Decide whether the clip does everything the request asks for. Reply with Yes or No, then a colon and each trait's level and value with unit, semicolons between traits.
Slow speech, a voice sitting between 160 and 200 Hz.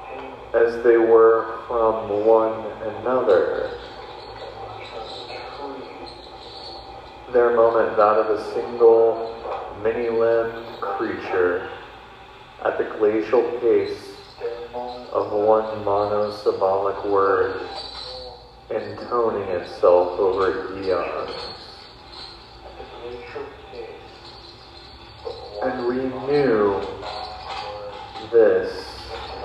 No: slow, 65 wpm; low, 135 Hz